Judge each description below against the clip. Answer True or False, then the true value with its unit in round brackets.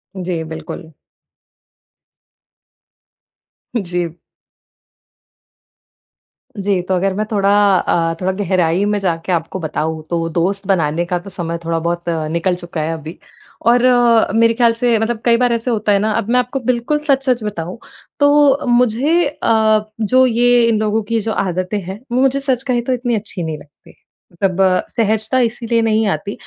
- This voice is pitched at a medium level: False (210 Hz)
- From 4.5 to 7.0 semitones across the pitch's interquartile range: True (5.2 semitones)